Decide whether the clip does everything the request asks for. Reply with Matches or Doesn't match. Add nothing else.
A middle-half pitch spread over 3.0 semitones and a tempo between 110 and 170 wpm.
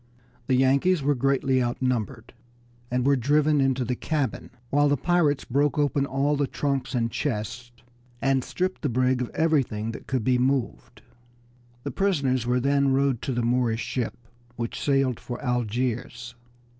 Doesn't match